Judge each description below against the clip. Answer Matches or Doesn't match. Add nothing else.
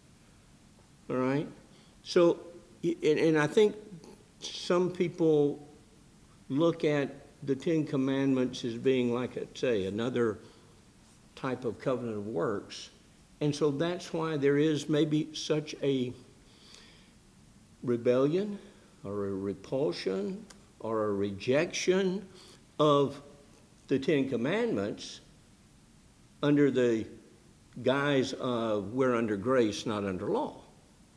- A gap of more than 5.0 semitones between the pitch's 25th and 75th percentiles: Matches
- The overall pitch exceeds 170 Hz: Doesn't match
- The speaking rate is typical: Doesn't match